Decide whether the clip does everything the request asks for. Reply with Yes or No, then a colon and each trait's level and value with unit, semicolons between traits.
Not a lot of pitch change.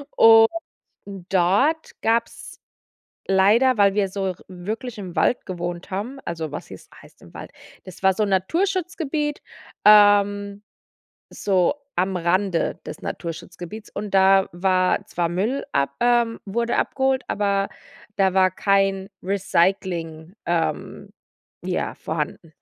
No: average, 3.4 semitones